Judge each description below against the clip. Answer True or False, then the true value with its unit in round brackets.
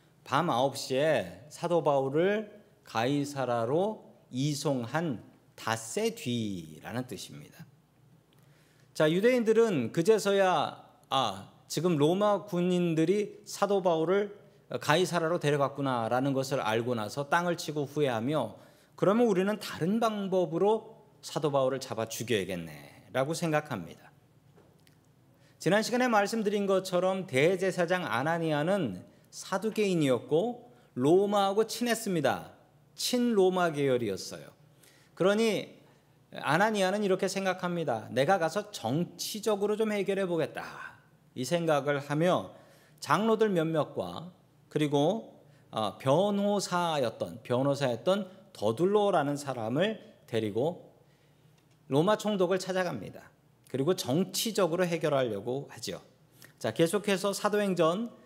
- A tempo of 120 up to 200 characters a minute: False (260 characters per minute)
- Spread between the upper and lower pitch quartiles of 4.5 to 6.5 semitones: True (5.5 semitones)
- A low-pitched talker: False (160 Hz)